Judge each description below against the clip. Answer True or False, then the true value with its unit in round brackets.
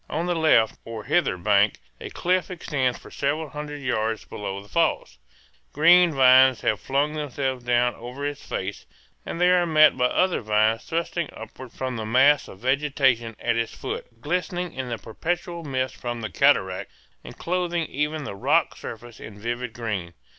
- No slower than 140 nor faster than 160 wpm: False (175 wpm)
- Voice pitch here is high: False (130 Hz)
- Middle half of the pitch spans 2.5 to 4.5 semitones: False (5.3 semitones)